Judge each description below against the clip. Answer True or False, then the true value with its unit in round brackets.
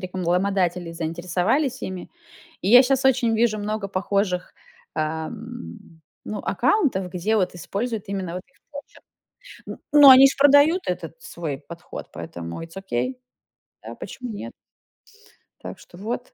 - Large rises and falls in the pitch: True (5.8 semitones)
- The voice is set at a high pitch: True (195 Hz)